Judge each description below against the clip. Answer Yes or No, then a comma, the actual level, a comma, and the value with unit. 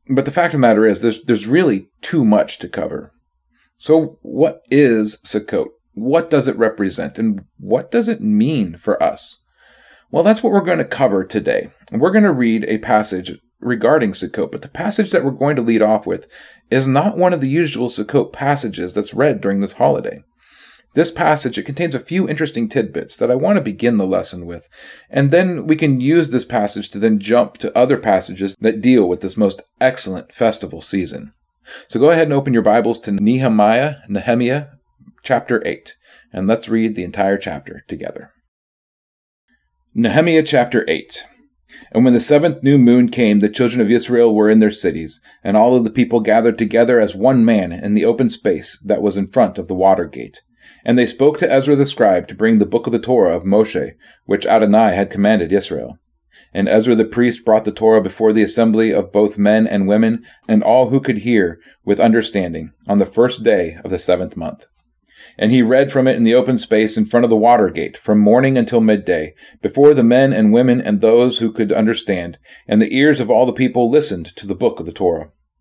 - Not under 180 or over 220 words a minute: Yes, fast, 205 wpm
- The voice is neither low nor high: No, low, 120 Hz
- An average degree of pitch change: Yes, average, 4.5 semitones